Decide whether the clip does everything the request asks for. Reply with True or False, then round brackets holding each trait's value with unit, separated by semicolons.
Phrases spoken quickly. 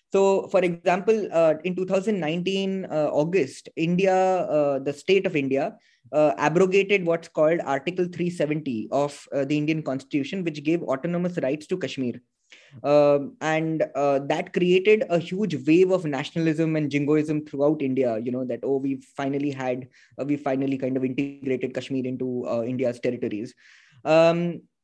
False (155 wpm)